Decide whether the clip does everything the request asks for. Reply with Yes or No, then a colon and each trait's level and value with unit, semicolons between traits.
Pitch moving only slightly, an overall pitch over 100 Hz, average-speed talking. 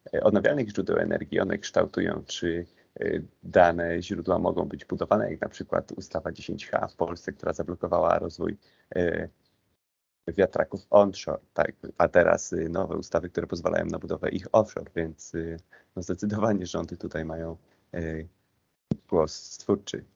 No: narrow, 2.1 semitones; very low, 85 Hz; average, 140 wpm